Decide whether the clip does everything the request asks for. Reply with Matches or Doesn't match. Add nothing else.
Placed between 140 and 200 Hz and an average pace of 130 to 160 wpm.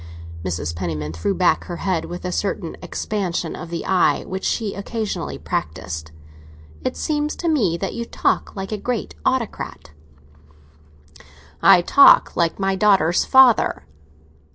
Matches